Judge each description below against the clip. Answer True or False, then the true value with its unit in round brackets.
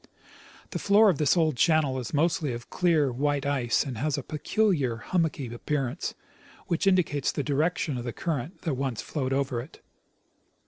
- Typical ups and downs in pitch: True (4.0 semitones)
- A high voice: False (145 Hz)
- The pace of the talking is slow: False (170 wpm)